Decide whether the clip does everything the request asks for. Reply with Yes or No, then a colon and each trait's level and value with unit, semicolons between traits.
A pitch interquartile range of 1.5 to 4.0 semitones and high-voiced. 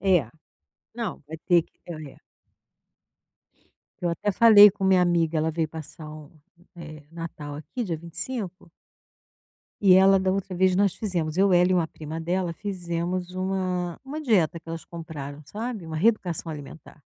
No: average, 3.1 semitones; medium, 175 Hz